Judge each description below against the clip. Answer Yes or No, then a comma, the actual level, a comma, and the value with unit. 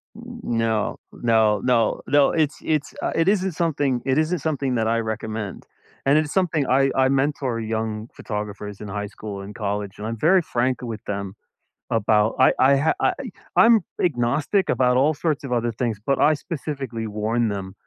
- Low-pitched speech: Yes, low, 120 Hz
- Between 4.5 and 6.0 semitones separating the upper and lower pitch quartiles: Yes, average, 5.0 semitones